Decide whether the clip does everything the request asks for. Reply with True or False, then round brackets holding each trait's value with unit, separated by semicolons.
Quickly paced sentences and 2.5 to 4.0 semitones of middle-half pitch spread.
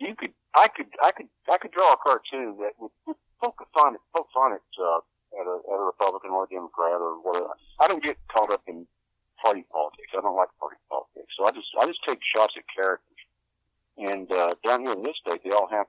False (235 wpm; 5.4 semitones)